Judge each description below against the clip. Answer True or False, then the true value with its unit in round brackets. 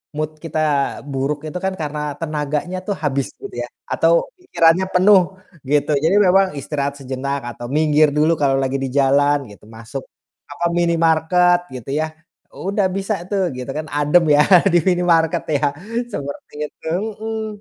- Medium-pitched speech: True (155 Hz)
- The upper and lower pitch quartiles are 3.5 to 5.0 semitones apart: True (4.0 semitones)